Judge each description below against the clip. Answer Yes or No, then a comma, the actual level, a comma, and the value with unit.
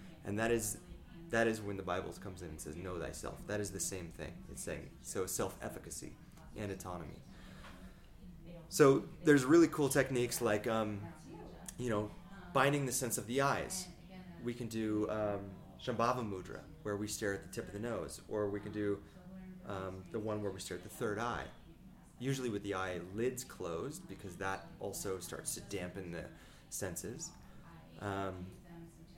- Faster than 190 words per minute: No, average, 175 wpm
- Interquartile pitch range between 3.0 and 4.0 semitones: No, average, 5.1 semitones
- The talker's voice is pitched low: Yes, low, 105 Hz